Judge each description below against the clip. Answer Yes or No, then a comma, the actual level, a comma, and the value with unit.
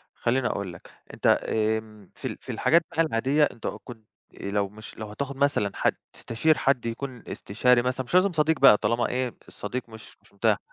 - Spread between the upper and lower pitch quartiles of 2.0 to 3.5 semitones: No, average, 4.2 semitones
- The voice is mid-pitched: No, low, 120 Hz